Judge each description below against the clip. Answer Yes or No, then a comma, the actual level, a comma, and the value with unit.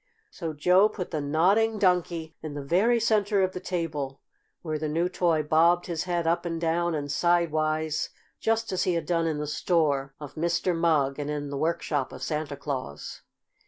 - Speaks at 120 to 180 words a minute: No, average, 190 wpm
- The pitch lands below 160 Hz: No, medium, 165 Hz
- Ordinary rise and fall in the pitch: Yes, average, 3.0 semitones